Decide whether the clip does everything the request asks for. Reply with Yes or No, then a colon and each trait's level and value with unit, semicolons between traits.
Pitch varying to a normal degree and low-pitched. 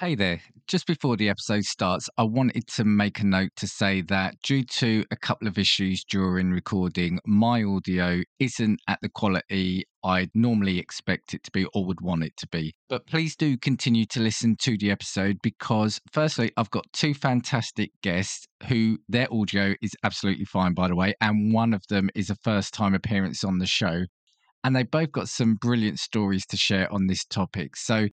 Yes: average, 3.5 semitones; low, 105 Hz